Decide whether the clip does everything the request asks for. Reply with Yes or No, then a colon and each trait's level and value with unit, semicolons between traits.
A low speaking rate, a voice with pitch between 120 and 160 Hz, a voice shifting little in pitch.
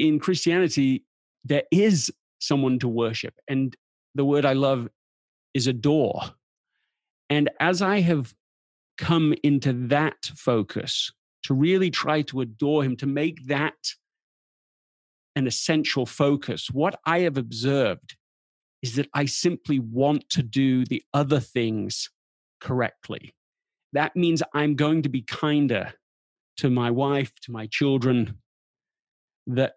No: slow, 125 wpm; medium, 140 Hz; average, 3.1 semitones